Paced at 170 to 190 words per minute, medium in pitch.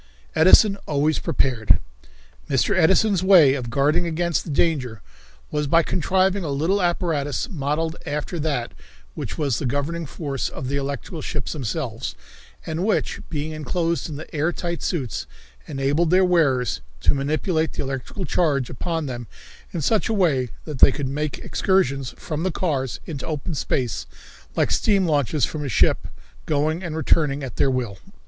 No: average, 160 wpm; medium, 150 Hz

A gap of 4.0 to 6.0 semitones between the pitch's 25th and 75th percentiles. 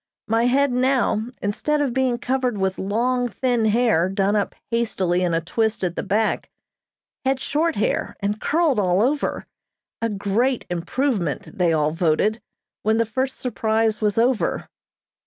Yes: average, 4.4 semitones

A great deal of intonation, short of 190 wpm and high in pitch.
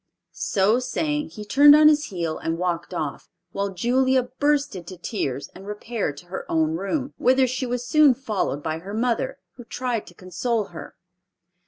Yes: wide, 6.5 semitones; average, 175 wpm; high, 220 Hz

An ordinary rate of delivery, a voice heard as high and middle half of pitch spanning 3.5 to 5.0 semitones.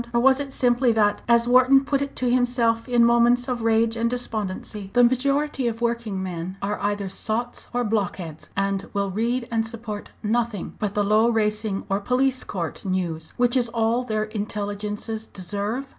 No: average, 180 wpm; high, 225 Hz; average, 3.0 semitones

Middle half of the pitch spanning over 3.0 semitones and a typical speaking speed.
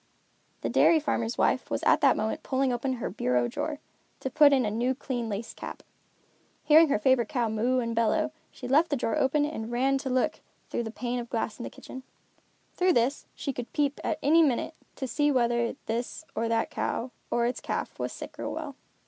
No: average, 3.4 semitones; fast, 210 wpm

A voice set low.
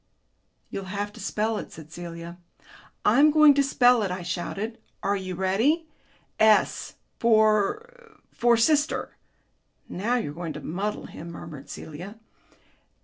No: high, 210 Hz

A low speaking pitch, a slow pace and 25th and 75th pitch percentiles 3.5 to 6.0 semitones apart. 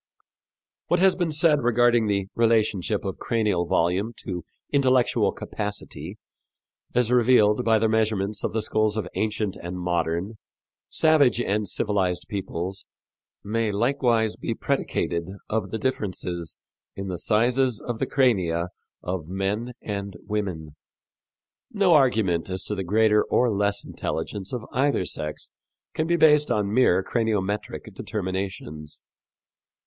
Yes: low, 105 Hz; slow, 130 wpm; average, 4.2 semitones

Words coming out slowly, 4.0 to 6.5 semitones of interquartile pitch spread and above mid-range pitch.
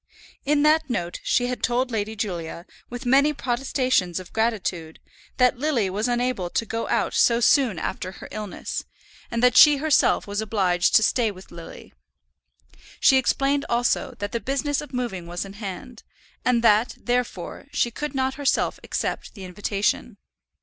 No: average, 165 wpm; average, 4.6 semitones; high, 235 Hz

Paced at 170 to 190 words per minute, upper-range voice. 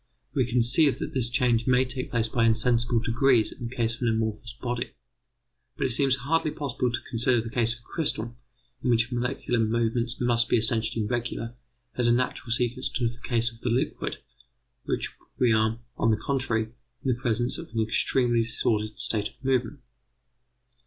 No: average, 180 wpm; low, 120 Hz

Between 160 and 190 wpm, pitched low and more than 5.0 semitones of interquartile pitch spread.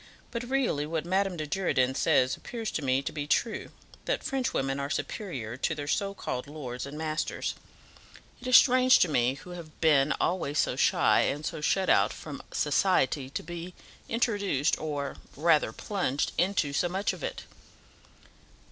No: average, 170 wpm; medium, 155 Hz; wide, 5.5 semitones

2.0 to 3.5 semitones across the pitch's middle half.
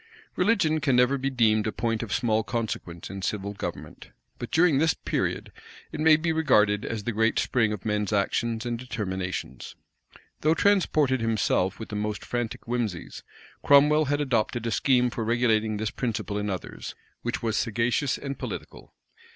No: average, 4.3 semitones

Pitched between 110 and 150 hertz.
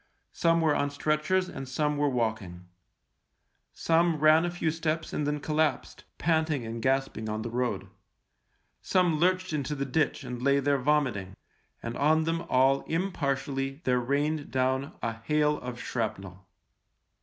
Yes: medium, 140 Hz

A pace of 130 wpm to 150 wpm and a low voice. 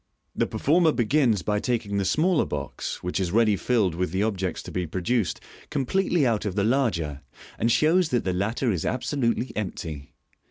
No: average, 175 wpm; low, 110 Hz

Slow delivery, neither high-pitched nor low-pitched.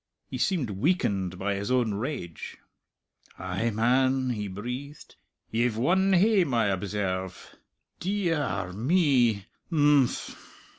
No: slow, 120 wpm; low, 120 Hz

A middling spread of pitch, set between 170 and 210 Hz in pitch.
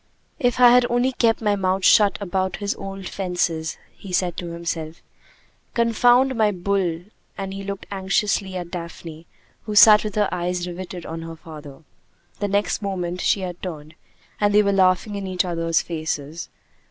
Yes: average, 3.2 semitones; high, 190 Hz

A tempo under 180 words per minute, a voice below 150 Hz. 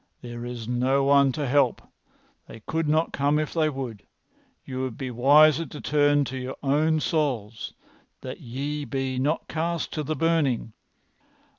Yes: average, 160 wpm; medium, 140 Hz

